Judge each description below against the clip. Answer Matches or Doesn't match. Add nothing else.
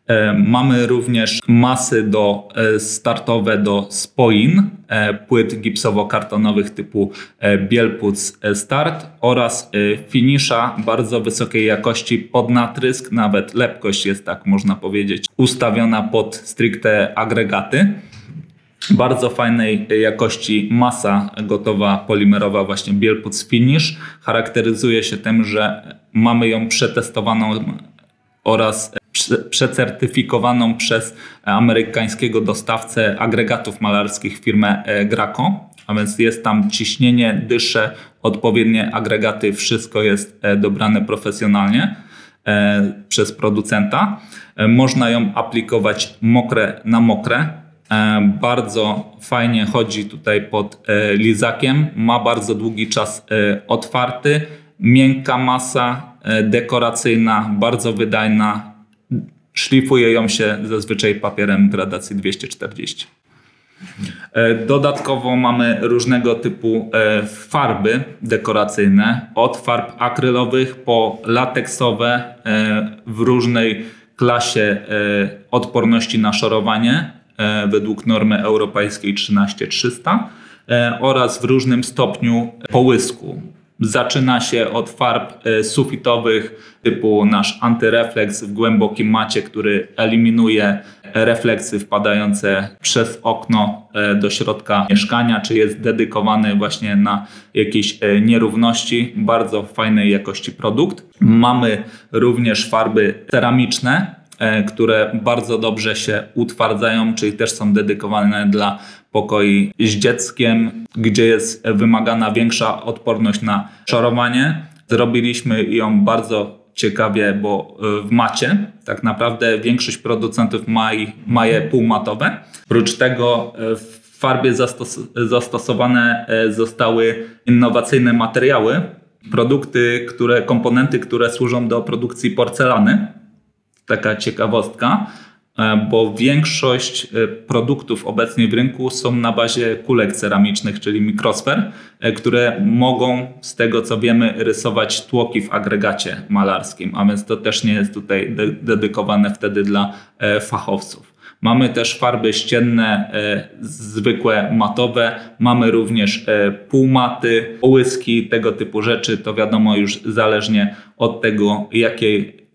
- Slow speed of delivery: Matches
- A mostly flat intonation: Matches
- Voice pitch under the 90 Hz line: Doesn't match